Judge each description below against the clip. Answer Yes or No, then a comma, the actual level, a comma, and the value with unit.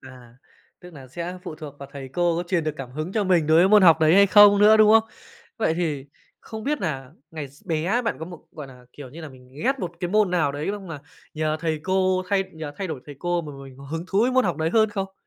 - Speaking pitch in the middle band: Yes, medium, 170 Hz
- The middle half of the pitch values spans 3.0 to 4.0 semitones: No, average, 4.7 semitones